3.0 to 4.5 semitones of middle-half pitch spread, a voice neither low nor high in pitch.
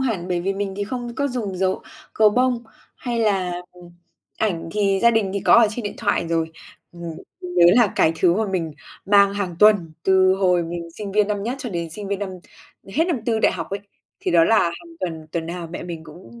No: average, 3.9 semitones; high, 195 Hz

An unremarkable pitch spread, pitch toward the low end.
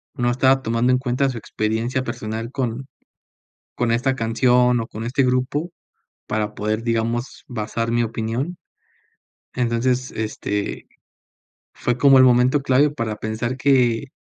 No: narrow, 2.3 semitones; low, 120 Hz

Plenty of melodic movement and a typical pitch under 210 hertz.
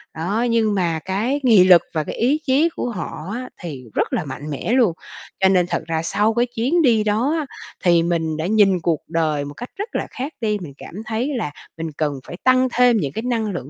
Yes: wide, 6.7 semitones; high, 200 Hz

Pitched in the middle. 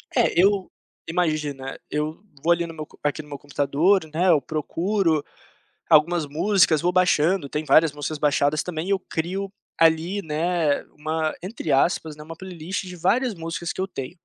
Yes: medium, 160 Hz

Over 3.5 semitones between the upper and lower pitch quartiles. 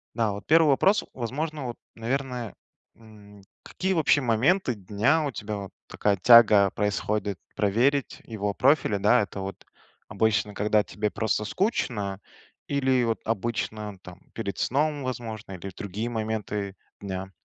Yes: average, 4.1 semitones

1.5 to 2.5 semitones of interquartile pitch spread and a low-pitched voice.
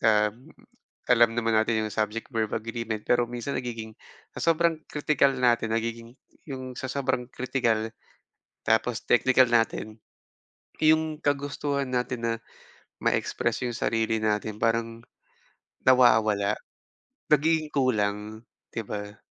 No: average, 2.9 semitones; low, 115 Hz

